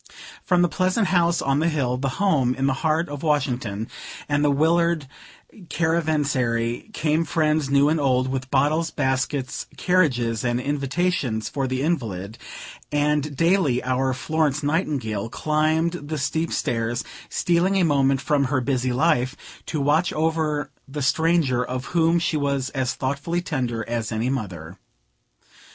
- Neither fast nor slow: Yes, average, 145 wpm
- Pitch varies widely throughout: No, average, 3.9 semitones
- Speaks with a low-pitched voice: No, medium, 145 Hz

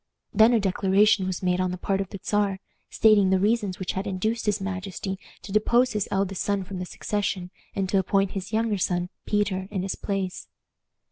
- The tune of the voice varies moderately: No, narrow, 1.8 semitones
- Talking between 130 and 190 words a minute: No, average, 200 wpm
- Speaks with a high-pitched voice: Yes, high, 195 Hz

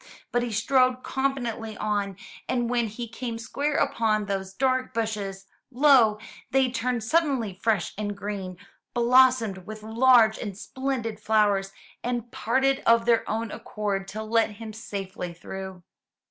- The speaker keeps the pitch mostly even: No, average, 3.3 semitones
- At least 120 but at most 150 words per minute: Yes, average, 140 wpm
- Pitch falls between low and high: No, high, 225 Hz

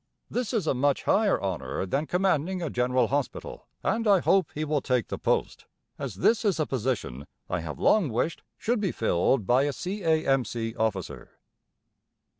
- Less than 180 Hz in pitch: Yes, medium, 140 Hz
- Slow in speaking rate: No, average, 170 wpm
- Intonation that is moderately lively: No, wide, 8.0 semitones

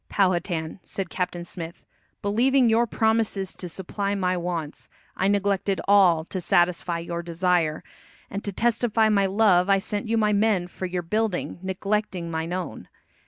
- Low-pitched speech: No, high, 190 Hz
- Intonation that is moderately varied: Yes, average, 3.1 semitones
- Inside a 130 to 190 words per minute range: Yes, average, 155 wpm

